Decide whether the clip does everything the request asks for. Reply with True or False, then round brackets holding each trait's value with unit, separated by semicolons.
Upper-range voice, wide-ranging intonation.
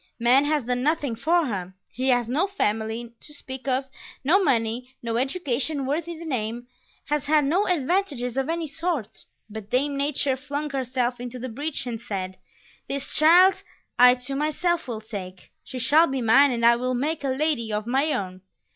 False (265 Hz; 4.1 semitones)